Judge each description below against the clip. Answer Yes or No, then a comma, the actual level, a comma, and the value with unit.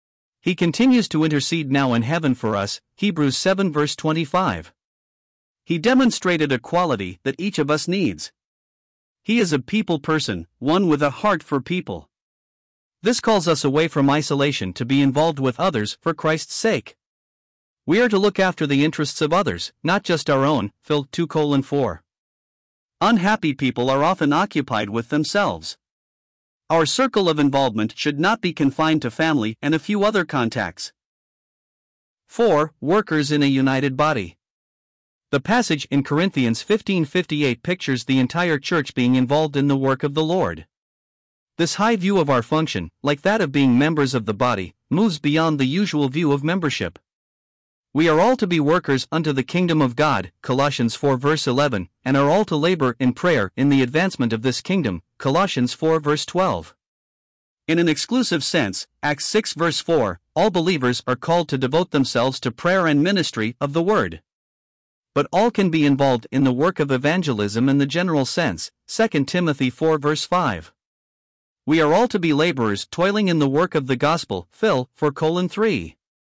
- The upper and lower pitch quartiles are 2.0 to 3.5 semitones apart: No, average, 5.3 semitones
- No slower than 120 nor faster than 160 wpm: No, average, 170 wpm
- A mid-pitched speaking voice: Yes, medium, 145 Hz